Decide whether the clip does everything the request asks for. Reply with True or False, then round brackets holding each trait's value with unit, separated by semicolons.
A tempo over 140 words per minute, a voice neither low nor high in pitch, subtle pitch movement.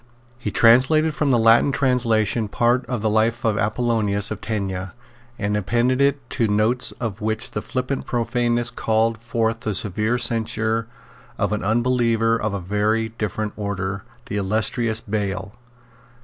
False (150 wpm; 110 Hz; 2.3 semitones)